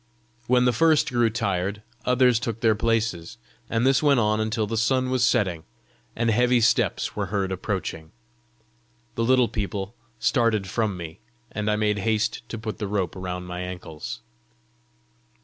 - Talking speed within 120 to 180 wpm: Yes, average, 160 wpm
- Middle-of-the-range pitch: No, low, 110 Hz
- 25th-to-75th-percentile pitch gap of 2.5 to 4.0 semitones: Yes, average, 3.5 semitones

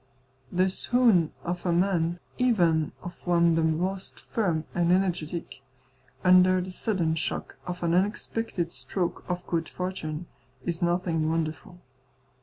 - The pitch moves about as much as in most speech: No, narrow, 2.0 semitones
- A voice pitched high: No, medium, 175 Hz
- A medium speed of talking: No, slow, 130 wpm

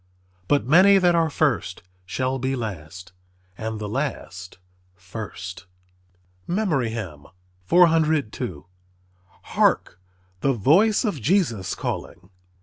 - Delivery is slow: Yes, slow, 95 wpm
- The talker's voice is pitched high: No, low, 115 Hz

